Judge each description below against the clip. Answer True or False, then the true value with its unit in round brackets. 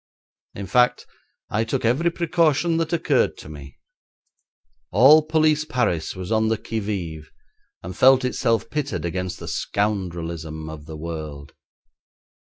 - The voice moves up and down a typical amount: False (8.6 semitones)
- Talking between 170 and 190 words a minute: False (135 wpm)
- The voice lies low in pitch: True (105 Hz)